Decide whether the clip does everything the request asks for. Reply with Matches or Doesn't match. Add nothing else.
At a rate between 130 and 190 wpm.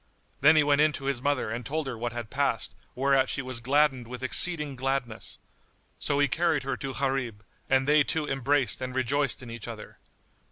Doesn't match